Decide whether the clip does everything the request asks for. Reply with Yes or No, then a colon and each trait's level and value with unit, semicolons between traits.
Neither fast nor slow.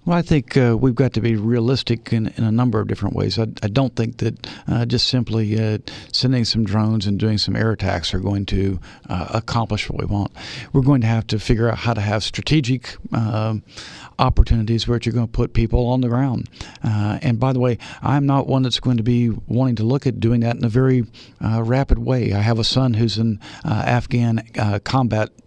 No: fast, 230 wpm